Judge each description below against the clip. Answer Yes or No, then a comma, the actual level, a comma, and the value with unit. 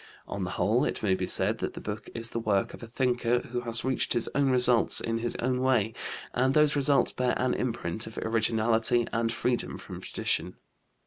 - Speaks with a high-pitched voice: No, low, 120 Hz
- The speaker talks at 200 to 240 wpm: Yes, fast, 205 wpm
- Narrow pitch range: Yes, narrow, 2.1 semitones